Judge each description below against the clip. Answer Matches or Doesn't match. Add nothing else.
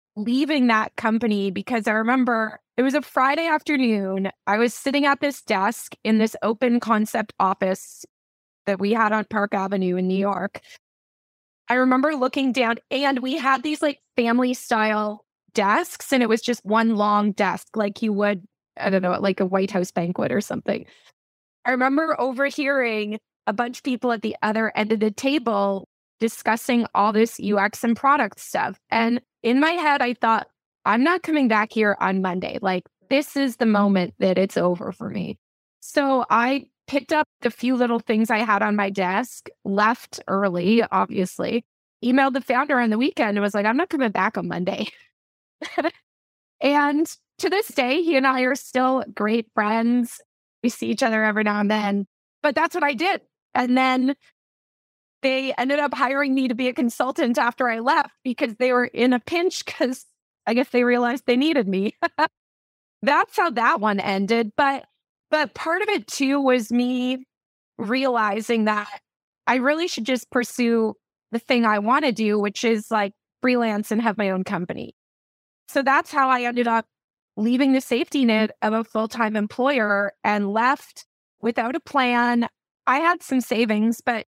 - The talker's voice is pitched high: Matches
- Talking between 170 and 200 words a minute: Matches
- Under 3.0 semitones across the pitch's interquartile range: Doesn't match